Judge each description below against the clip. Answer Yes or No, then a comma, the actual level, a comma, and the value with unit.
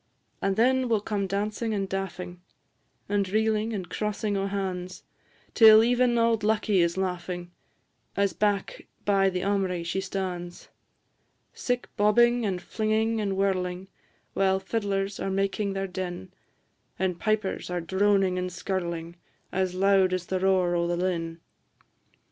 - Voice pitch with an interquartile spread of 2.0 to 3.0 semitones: Yes, narrow, 2.5 semitones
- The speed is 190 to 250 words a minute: No, average, 140 wpm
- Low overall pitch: No, high, 195 Hz